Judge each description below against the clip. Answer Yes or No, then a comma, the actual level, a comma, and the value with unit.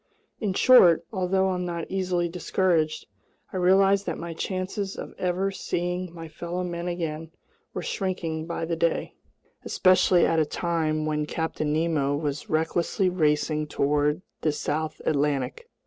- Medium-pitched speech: Yes, medium, 170 Hz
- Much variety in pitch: No, average, 3.0 semitones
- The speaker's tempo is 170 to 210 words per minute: No, average, 145 wpm